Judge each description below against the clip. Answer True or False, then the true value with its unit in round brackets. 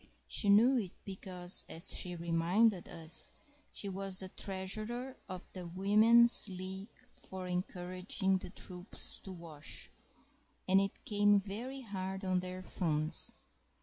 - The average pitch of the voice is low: False (190 Hz)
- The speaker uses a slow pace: True (120 wpm)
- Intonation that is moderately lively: False (2.2 semitones)